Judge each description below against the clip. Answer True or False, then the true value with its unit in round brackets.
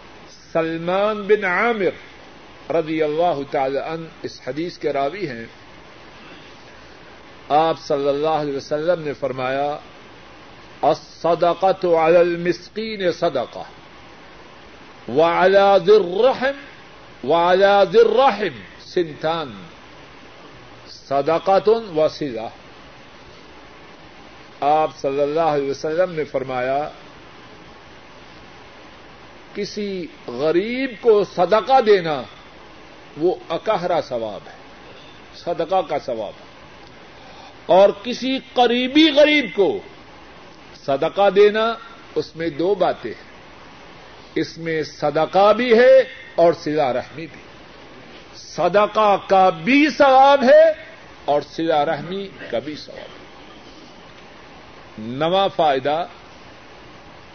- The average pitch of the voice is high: False (175 Hz)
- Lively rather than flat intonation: True (6.0 semitones)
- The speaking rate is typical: False (90 wpm)